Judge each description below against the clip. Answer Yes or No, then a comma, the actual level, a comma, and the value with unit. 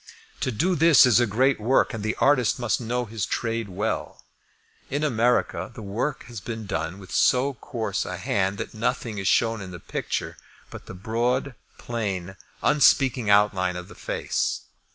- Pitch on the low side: Yes, low, 115 Hz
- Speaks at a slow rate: No, average, 175 wpm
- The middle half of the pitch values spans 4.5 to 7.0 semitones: No, average, 3.8 semitones